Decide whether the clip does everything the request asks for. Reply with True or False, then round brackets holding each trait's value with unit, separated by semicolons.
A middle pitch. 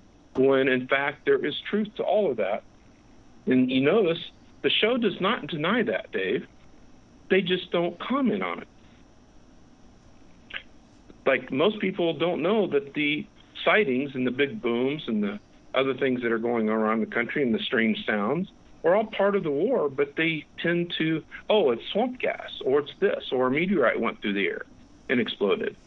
True (175 Hz)